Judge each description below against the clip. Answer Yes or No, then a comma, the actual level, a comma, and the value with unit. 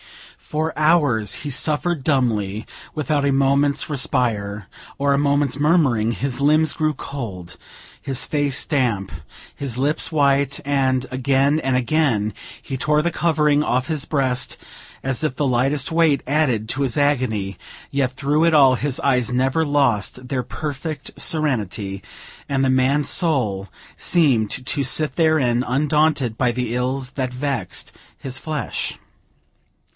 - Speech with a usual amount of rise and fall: Yes, average, 3.0 semitones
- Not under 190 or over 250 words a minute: No, average, 140 wpm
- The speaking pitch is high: No, low, 135 Hz